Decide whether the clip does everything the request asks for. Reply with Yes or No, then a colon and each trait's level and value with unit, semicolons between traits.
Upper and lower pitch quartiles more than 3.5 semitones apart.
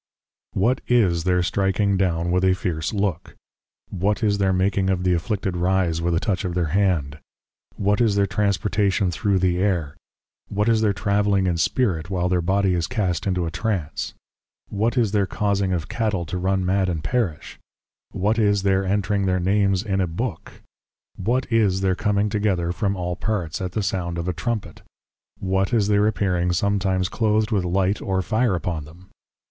No: narrow, 2.4 semitones